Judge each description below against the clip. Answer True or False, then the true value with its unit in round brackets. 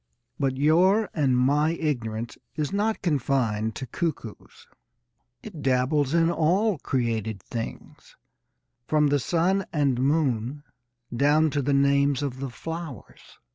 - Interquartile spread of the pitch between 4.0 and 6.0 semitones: True (4.3 semitones)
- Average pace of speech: False (125 wpm)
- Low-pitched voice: False (145 Hz)